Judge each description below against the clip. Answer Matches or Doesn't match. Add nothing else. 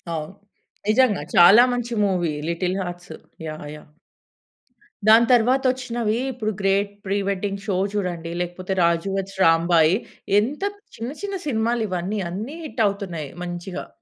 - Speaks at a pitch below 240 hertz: Matches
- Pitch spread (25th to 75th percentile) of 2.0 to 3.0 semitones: Doesn't match